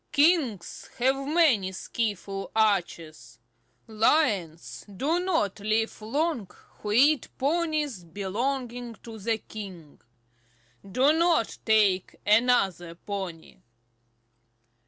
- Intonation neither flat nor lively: No, wide, 6.0 semitones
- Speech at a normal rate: No, slow, 90 wpm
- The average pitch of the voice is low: No, high, 220 Hz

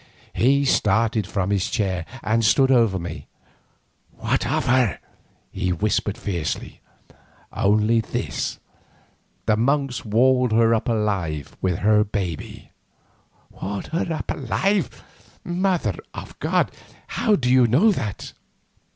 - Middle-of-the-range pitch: No, low, 110 Hz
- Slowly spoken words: Yes, slow, 120 wpm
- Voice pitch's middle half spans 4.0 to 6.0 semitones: Yes, average, 4.5 semitones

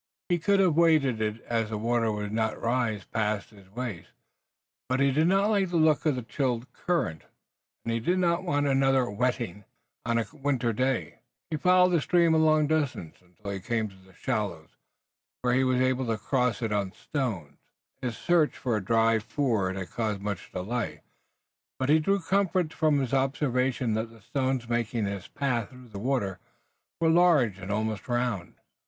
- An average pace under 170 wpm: No, average, 185 wpm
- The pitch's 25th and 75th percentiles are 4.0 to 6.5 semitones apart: Yes, average, 5.3 semitones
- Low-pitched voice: Yes, low, 125 Hz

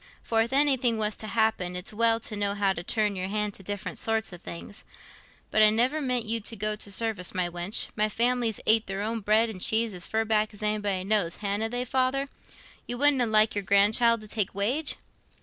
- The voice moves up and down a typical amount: No, narrow, 2.3 semitones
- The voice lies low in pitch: No, high, 215 Hz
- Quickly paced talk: Yes, fast, 220 wpm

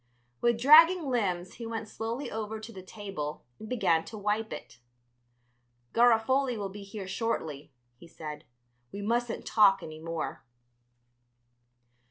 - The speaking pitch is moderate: No, high, 215 Hz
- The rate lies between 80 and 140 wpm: Yes, slow, 135 wpm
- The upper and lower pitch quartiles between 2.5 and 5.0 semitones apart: Yes, average, 3.8 semitones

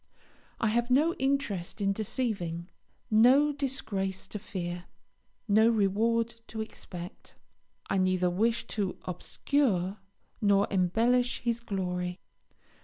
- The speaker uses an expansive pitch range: No, average, 4.2 semitones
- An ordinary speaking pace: No, slow, 110 wpm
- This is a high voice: Yes, high, 210 Hz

